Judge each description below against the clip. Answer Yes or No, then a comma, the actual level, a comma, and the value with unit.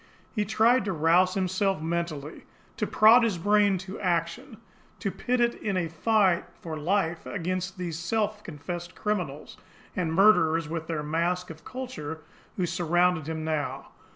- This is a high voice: No, medium, 180 Hz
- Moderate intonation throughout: Yes, average, 3.9 semitones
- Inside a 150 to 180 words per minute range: Yes, average, 155 wpm